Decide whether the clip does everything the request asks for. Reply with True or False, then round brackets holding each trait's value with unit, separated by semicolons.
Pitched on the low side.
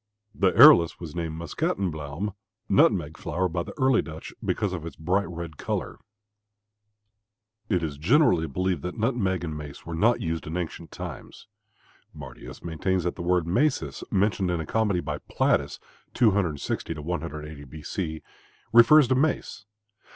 True (85 Hz)